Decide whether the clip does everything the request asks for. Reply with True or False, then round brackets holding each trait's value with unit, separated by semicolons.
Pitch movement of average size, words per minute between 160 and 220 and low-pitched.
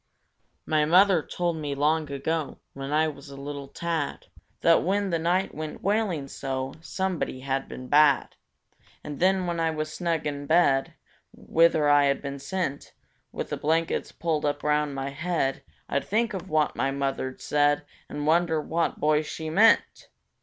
False (3.1 semitones; 165 wpm; 155 Hz)